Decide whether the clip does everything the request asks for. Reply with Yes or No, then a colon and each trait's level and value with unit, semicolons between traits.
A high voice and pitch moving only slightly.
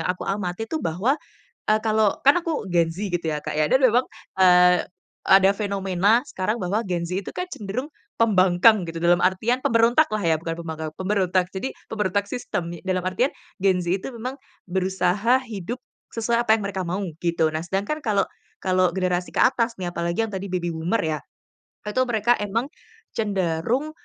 No: high, 195 Hz; average, 4.1 semitones